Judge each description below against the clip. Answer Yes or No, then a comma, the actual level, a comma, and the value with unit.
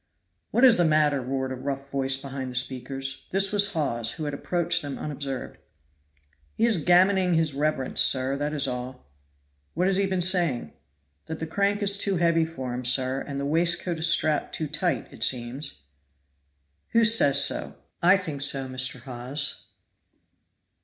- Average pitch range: Yes, average, 4.7 semitones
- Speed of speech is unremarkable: Yes, average, 170 wpm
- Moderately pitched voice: Yes, medium, 145 Hz